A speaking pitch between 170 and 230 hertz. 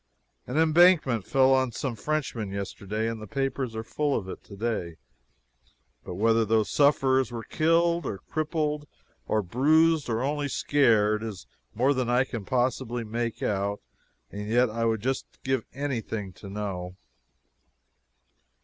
No: low, 120 Hz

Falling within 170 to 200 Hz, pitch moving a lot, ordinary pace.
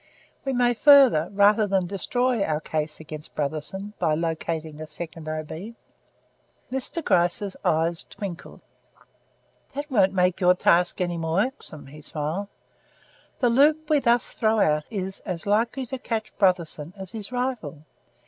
Yes: high, 190 Hz; wide, 6.5 semitones; average, 145 wpm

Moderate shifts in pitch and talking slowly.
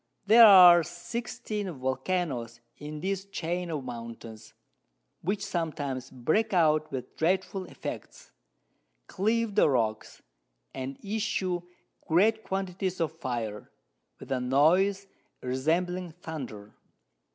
No: wide, 6.7 semitones; slow, 105 wpm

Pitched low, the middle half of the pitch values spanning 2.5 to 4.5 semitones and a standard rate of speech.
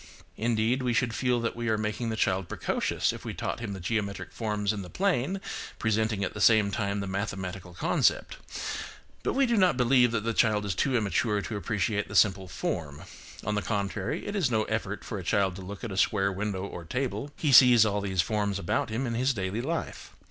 No: low, 105 Hz; average, 3.2 semitones; fast, 220 wpm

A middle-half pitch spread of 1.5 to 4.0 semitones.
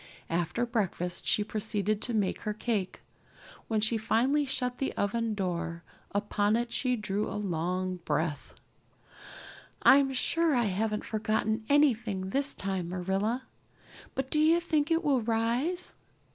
No: average, 4.6 semitones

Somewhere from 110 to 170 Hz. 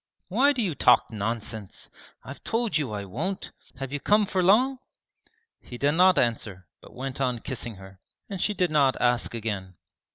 Yes: low, 135 Hz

